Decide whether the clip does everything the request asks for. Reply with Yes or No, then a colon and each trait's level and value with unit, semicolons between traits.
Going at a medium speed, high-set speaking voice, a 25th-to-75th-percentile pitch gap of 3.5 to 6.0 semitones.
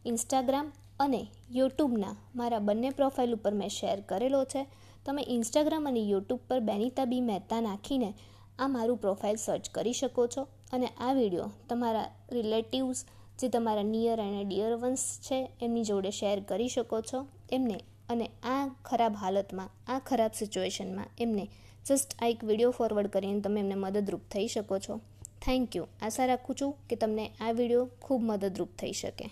No: fast, 160 wpm; high, 230 Hz; average, 3.9 semitones